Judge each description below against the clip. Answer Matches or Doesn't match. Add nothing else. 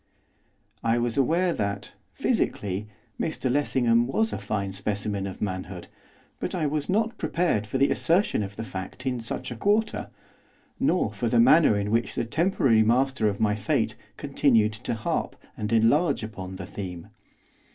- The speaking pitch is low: Matches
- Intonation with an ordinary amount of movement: Doesn't match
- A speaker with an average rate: Matches